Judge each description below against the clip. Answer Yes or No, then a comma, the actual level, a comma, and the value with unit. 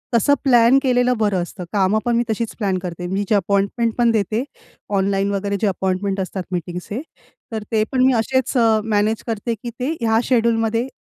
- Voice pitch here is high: Yes, high, 220 Hz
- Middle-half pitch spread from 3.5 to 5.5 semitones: No, average, 3.0 semitones